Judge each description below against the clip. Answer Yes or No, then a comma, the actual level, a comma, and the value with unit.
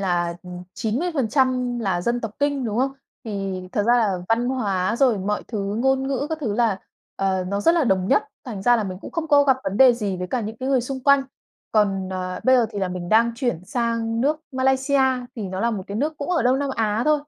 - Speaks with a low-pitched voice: No, high, 230 Hz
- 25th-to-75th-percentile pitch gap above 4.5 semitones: Yes, average, 5.1 semitones